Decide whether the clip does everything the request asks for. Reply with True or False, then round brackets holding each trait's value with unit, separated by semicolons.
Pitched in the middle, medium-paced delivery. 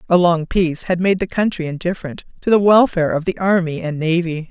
False (175 Hz; 215 wpm)